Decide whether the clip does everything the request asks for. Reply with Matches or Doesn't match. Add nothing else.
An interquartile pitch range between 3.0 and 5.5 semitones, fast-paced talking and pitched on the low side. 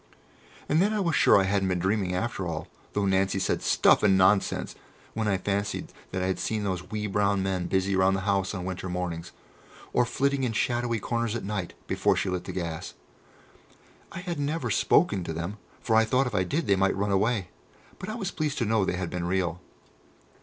Matches